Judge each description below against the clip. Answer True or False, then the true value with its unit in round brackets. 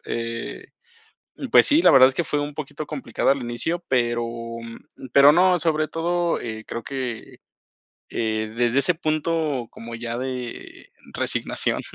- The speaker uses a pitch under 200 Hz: True (135 Hz)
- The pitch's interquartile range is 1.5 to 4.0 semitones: False (4.9 semitones)